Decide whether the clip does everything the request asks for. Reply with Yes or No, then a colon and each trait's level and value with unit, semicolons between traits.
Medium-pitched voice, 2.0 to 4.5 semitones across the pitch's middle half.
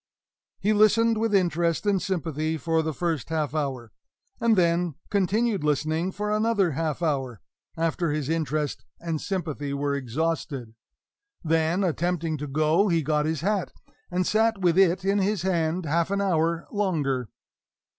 Yes: medium, 165 Hz; average, 4.0 semitones